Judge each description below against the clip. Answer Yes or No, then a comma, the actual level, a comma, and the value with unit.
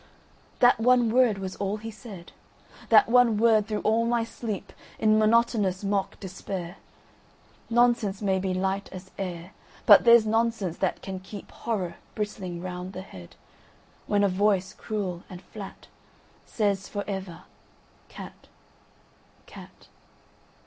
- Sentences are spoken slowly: Yes, slow, 115 wpm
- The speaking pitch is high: Yes, high, 200 Hz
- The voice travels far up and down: No, average, 3.0 semitones